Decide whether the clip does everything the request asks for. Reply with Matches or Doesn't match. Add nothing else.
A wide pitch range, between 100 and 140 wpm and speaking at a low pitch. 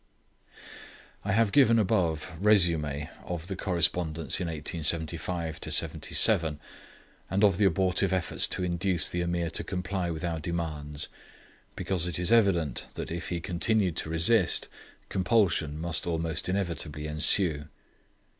Doesn't match